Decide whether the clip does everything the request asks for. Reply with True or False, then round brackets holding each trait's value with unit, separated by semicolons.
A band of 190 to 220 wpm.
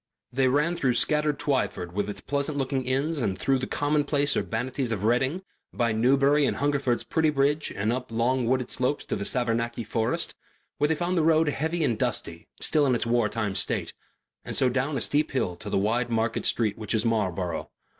True (195 wpm)